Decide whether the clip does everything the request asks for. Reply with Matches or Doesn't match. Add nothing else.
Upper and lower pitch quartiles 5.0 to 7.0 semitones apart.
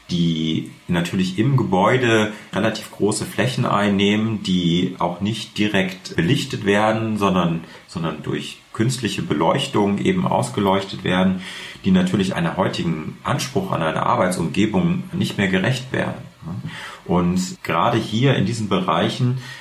Matches